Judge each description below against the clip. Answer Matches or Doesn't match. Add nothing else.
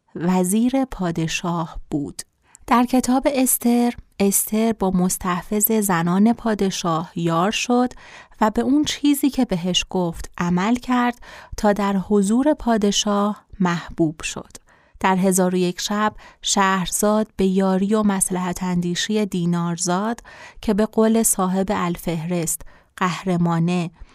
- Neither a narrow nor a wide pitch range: Matches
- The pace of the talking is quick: Doesn't match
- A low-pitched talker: Doesn't match